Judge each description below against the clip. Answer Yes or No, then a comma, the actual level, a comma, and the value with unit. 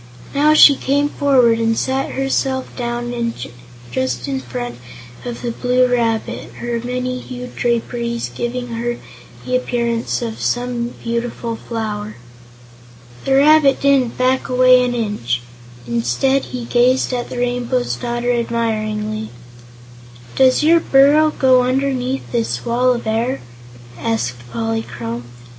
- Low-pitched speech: No, high, 240 Hz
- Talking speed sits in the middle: No, slow, 125 wpm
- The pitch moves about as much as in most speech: No, narrow, 2.1 semitones